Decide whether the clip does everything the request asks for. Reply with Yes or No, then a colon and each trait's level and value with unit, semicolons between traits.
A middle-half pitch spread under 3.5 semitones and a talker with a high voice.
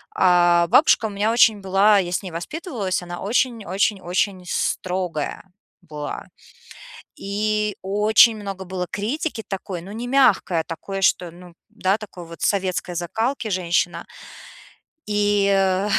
Yes: average, 3.0 semitones; high, 195 Hz